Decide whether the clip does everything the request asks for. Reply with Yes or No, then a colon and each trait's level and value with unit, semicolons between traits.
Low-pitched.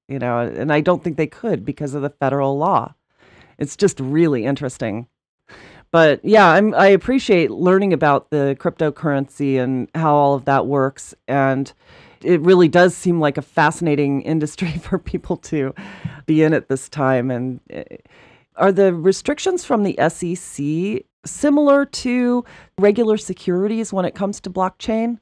No: medium, 165 Hz